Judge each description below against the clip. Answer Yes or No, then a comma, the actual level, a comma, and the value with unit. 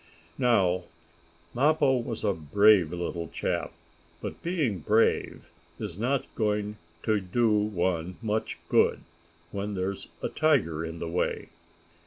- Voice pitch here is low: Yes, low, 105 Hz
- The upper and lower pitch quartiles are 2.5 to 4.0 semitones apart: No, average, 4.6 semitones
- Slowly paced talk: Yes, slow, 125 wpm